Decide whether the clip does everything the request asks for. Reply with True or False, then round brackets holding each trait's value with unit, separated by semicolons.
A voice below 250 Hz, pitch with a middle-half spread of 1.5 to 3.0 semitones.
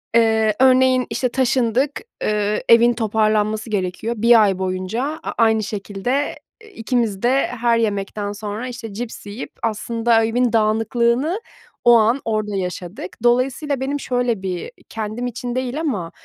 True (230 Hz; 2.7 semitones)